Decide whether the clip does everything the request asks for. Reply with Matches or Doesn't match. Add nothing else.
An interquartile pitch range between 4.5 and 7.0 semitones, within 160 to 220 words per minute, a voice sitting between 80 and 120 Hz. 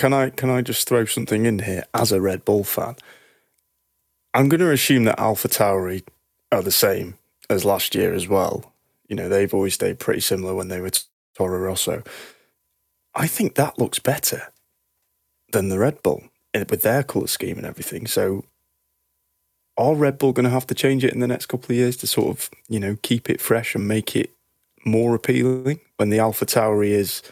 Matches